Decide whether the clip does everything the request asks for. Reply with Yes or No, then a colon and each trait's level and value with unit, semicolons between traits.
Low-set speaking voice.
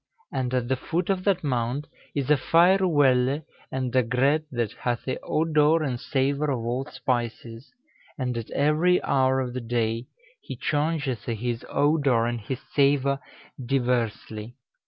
Yes: low, 130 Hz